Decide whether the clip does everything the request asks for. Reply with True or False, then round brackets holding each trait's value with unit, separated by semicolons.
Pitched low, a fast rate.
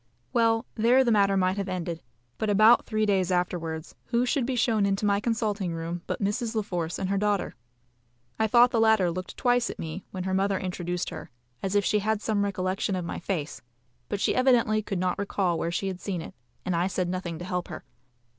False (195 Hz; 220 wpm)